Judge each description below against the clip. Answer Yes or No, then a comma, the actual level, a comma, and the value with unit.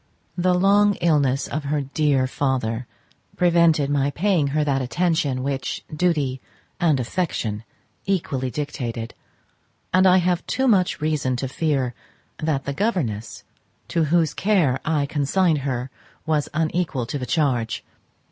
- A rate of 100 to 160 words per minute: Yes, slow, 135 wpm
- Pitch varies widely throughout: No, average, 4.5 semitones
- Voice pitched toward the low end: No, medium, 150 Hz